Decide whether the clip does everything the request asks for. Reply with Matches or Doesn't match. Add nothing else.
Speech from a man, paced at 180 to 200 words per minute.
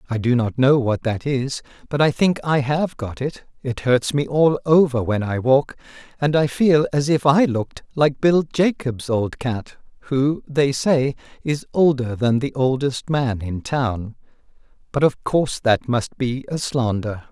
Matches